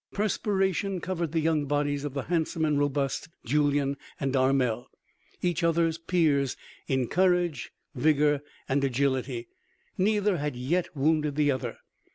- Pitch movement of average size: Yes, average, 3.6 semitones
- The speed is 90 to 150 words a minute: Yes, slow, 135 wpm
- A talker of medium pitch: Yes, medium, 150 Hz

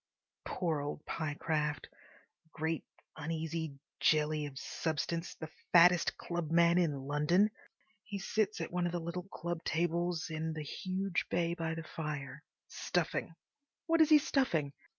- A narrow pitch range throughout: Yes, narrow, 2.3 semitones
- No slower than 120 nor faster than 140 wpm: Yes, slow, 135 wpm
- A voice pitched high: No, medium, 165 Hz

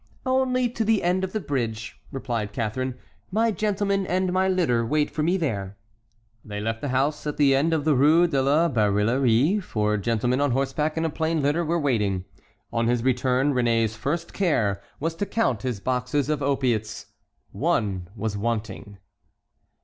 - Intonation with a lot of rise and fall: Yes, wide, 6.6 semitones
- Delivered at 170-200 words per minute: Yes, average, 175 wpm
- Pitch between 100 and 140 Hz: Yes, low, 135 Hz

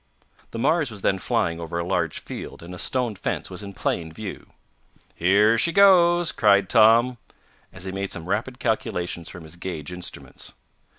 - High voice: No, low, 100 Hz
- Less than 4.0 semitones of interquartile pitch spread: No, average, 5.1 semitones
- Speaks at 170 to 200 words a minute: Yes, average, 175 wpm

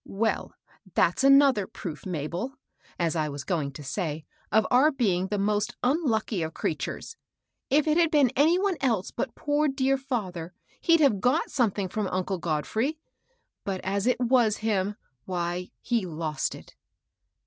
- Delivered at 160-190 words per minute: Yes, average, 170 wpm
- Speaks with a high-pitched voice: Yes, high, 210 Hz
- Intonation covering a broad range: Yes, wide, 7.3 semitones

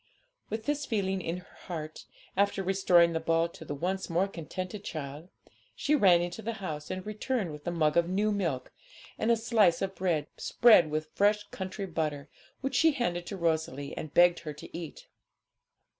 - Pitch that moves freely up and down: No, average, 4.0 semitones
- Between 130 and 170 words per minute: No, average, 185 wpm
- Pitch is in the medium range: Yes, medium, 175 Hz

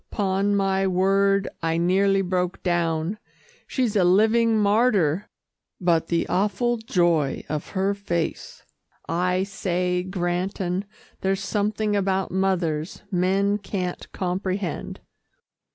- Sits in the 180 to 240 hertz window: Yes, high, 190 Hz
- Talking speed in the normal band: No, slow, 105 wpm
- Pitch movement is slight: Yes, narrow, 2.2 semitones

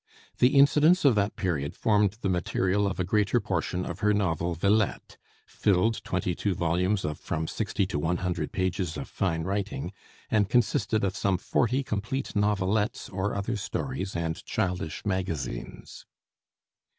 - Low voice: Yes, very low, 95 Hz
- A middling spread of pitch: Yes, average, 3.0 semitones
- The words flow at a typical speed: Yes, average, 150 wpm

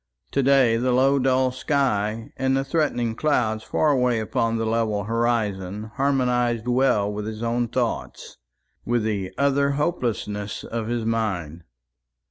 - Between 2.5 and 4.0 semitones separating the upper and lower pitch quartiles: Yes, average, 3.4 semitones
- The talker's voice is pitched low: Yes, low, 115 Hz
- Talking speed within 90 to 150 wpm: Yes, average, 140 wpm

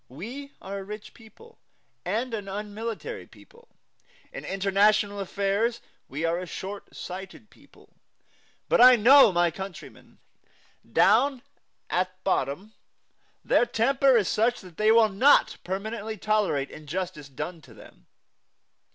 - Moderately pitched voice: No, high, 205 Hz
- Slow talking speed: Yes, slow, 125 wpm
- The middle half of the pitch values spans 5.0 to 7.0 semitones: No, average, 3.8 semitones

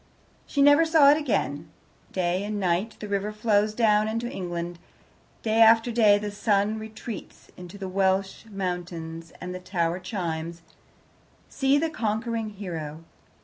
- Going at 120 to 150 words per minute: Yes, average, 145 wpm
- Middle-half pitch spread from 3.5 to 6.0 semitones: Yes, average, 3.9 semitones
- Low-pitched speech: No, high, 205 Hz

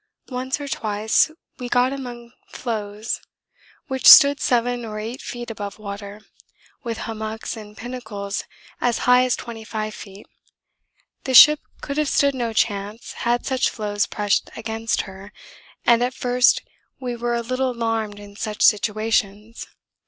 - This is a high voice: Yes, high, 230 Hz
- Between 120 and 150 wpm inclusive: Yes, average, 145 wpm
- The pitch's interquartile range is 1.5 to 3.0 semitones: Yes, average, 2.7 semitones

